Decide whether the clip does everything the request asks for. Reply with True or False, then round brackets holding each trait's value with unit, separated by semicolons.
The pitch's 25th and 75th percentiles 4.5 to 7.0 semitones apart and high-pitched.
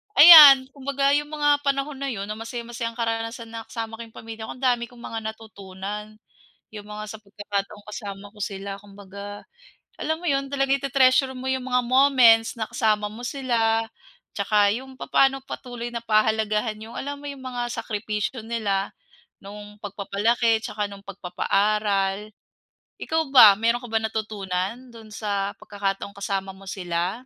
False (3.7 semitones; 225 Hz)